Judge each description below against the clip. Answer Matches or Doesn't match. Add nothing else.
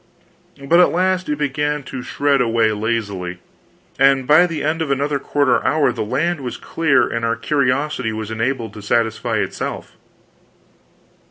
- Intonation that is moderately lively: Matches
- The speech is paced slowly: Doesn't match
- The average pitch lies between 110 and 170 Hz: Matches